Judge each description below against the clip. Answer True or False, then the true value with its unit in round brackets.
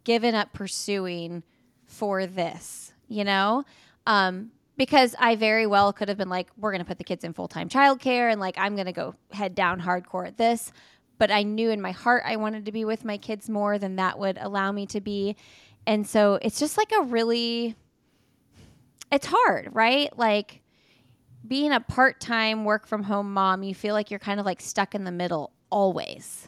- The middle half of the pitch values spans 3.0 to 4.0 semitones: True (3.3 semitones)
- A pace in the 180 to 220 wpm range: True (190 wpm)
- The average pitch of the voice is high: True (205 Hz)